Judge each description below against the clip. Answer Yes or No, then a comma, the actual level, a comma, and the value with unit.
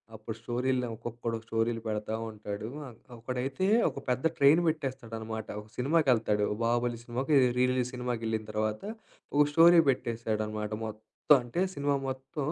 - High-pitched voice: No, low, 120 Hz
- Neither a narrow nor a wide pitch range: Yes, average, 3.0 semitones